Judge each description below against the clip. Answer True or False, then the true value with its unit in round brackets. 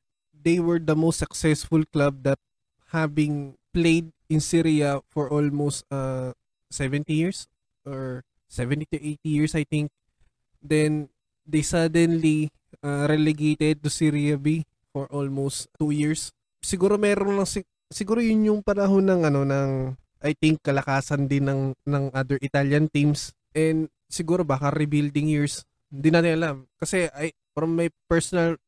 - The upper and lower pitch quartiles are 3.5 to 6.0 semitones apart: False (2.7 semitones)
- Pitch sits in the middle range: True (150 Hz)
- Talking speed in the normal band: True (145 wpm)